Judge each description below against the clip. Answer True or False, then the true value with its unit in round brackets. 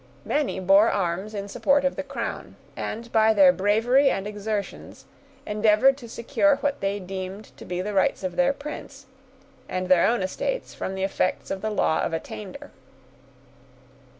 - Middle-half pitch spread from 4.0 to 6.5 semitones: True (5.6 semitones)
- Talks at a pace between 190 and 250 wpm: False (165 wpm)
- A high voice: True (210 Hz)